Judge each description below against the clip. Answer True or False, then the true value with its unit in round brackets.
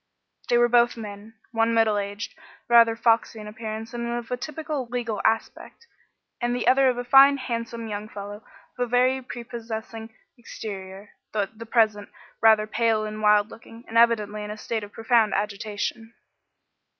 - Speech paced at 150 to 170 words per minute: True (160 wpm)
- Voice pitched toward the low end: False (225 Hz)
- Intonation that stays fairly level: True (2.0 semitones)